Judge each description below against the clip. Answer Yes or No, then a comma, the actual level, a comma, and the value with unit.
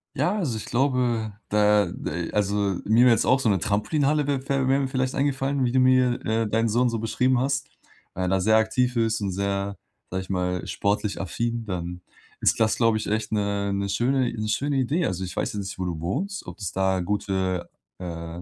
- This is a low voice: Yes, low, 110 Hz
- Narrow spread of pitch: No, average, 4.7 semitones